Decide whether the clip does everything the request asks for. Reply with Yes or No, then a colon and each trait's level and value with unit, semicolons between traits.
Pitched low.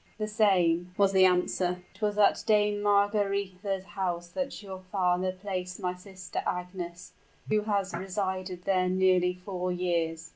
No: medium, 185 Hz